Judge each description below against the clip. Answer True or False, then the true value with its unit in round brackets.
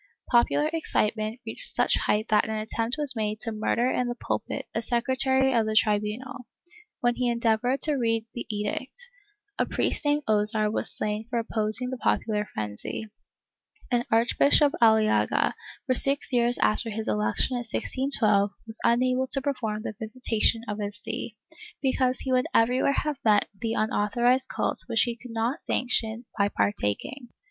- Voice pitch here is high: True (230 Hz)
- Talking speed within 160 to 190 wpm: True (165 wpm)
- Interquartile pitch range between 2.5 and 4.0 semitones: True (2.9 semitones)